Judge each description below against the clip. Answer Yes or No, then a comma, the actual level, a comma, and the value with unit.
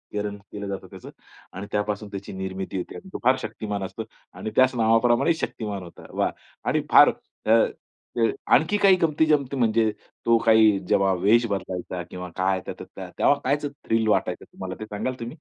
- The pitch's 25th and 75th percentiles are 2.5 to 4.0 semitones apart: Yes, average, 3.3 semitones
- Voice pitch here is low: Yes, low, 110 Hz